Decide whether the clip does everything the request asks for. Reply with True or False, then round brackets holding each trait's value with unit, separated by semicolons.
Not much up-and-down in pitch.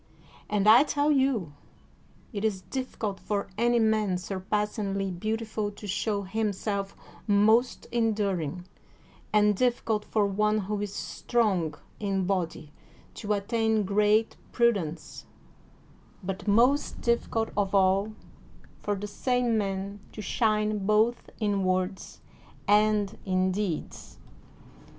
True (2.2 semitones)